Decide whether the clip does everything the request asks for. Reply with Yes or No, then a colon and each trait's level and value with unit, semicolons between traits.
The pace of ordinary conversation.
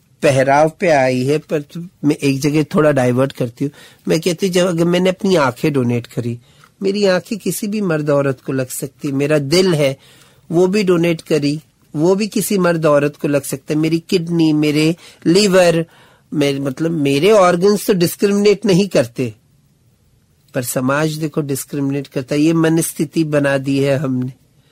Yes: average, 170 wpm